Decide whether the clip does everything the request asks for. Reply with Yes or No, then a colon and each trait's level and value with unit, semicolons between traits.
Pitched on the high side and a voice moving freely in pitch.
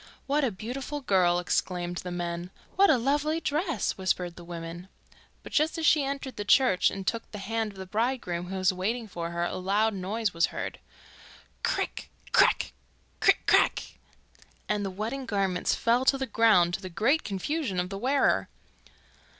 Yes: high, 205 Hz; wide, 6.5 semitones